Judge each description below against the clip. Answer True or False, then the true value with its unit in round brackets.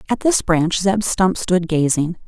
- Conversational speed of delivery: True (185 wpm)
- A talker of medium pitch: True (180 Hz)